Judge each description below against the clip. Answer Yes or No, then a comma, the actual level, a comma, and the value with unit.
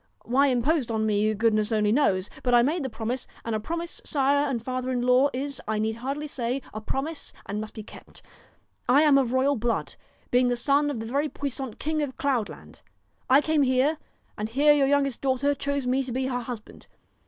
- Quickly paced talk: Yes, fast, 215 wpm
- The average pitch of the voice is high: Yes, very high, 260 Hz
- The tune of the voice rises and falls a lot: No, average, 3.5 semitones